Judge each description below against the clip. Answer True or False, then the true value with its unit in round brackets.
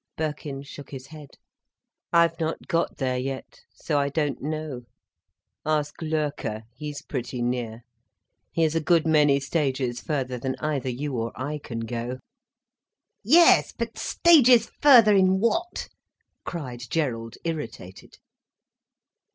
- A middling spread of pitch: True (4.3 semitones)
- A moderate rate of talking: False (125 wpm)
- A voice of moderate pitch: True (145 Hz)